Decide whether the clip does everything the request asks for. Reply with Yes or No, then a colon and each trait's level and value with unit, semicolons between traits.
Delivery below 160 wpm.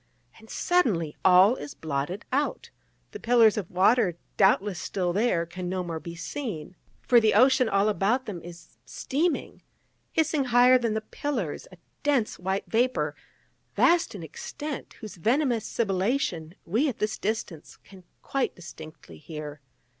Yes: average, 145 wpm